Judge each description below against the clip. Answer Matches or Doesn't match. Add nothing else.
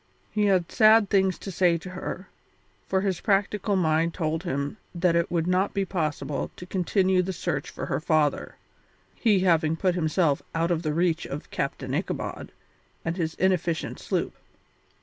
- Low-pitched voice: Doesn't match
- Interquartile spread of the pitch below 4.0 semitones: Matches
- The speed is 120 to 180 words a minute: Matches